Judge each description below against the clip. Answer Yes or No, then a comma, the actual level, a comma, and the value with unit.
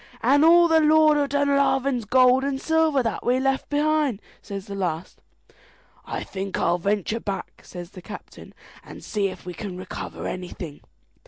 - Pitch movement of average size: No, wide, 6.7 semitones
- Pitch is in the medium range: No, very high, 250 Hz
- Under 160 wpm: No, average, 165 wpm